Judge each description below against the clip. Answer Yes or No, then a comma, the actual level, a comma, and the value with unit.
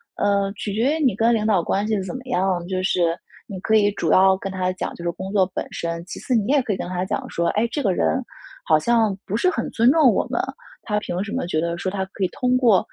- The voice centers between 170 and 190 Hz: No, high, 200 Hz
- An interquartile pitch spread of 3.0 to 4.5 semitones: Yes, average, 3.8 semitones